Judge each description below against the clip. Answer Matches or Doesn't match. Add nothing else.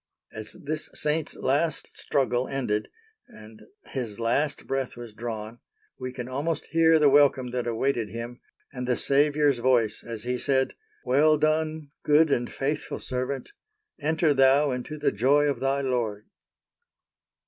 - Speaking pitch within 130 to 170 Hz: Matches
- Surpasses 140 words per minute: Doesn't match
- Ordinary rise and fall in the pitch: Matches